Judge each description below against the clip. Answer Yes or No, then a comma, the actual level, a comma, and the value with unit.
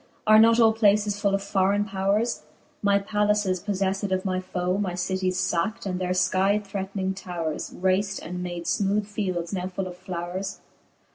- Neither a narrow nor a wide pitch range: No, narrow, 1.8 semitones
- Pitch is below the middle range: No, high, 195 Hz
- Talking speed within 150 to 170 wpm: Yes, average, 165 wpm